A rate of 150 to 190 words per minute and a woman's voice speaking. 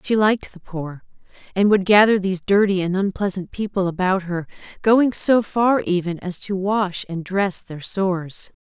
Yes: average, 175 wpm; female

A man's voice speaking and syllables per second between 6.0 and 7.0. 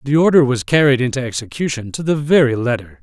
Yes: male; 6.2 syllables/s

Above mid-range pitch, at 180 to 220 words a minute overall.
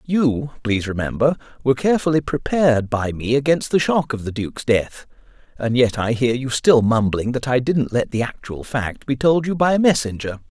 No: low, 130 Hz; average, 200 wpm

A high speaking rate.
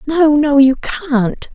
No: average, 155 wpm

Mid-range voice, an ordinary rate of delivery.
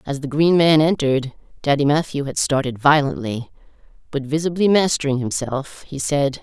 Yes: medium, 145 Hz; average, 150 wpm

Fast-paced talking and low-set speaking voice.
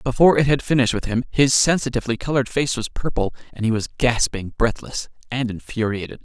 No: average, 175 wpm; low, 125 Hz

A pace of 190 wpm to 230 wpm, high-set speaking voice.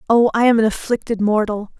Yes: average, 200 wpm; high, 220 Hz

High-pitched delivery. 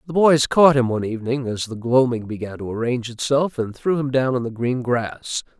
No: low, 125 Hz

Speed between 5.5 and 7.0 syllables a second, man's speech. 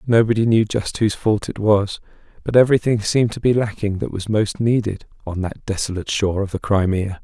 Yes: 5.8 syllables/s; male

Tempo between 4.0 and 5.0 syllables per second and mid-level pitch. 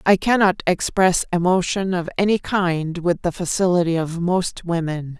Yes: 4.5 syllables/s; medium, 175 Hz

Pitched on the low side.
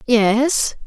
No: high, 240 Hz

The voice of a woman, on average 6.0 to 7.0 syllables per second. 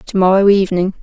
Yes: female; 6.8 syllables/s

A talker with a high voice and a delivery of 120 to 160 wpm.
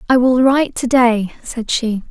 No: high, 245 Hz; average, 200 wpm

